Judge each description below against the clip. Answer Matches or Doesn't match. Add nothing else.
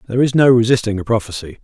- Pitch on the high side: Doesn't match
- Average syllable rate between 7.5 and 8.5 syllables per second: Matches